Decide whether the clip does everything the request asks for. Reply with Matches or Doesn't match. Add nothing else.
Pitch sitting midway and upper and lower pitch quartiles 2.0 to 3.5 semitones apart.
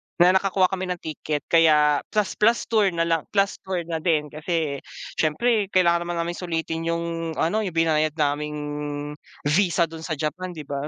Matches